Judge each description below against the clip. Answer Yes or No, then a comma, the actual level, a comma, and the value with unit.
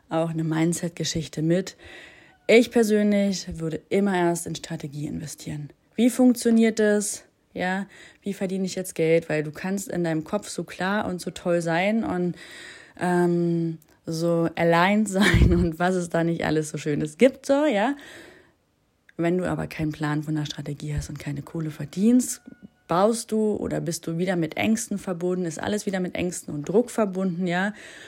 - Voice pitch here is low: No, medium, 180 Hz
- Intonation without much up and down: No, average, 4.3 semitones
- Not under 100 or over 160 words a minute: No, average, 175 wpm